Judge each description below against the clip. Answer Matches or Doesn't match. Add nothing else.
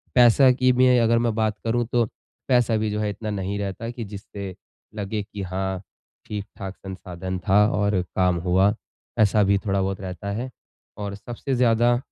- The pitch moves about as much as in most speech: Matches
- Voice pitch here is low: Matches